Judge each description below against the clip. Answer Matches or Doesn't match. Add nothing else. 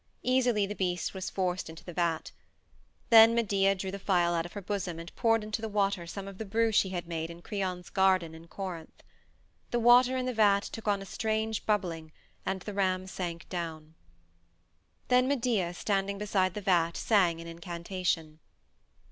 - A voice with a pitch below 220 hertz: Matches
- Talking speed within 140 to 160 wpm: Doesn't match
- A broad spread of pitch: Doesn't match